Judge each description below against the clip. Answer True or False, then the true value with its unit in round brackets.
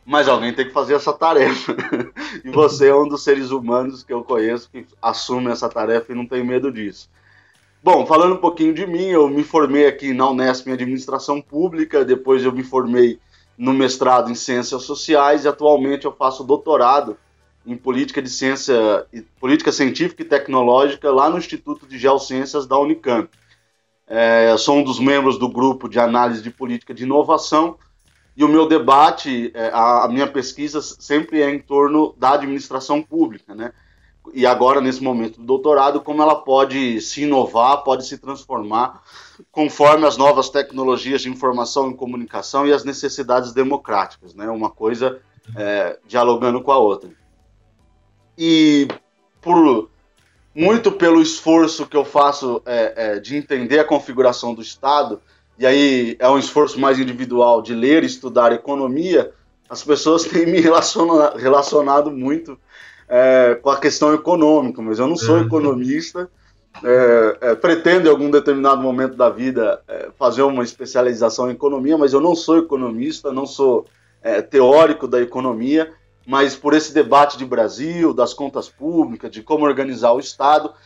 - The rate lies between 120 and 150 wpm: False (165 wpm)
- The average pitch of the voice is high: False (135 Hz)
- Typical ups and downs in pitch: True (3.4 semitones)